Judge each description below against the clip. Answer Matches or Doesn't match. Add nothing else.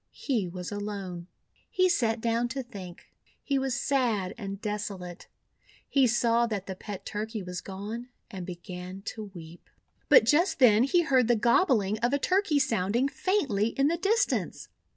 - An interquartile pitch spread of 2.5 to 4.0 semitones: Doesn't match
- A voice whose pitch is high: Matches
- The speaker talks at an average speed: Matches